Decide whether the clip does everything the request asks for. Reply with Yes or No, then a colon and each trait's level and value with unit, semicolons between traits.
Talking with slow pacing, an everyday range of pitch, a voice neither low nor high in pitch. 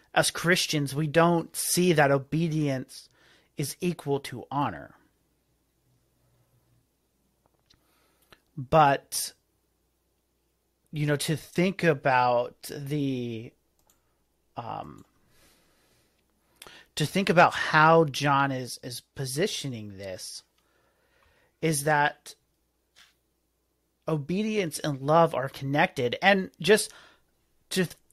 Yes: slow, 85 wpm; average, 4.2 semitones; medium, 150 Hz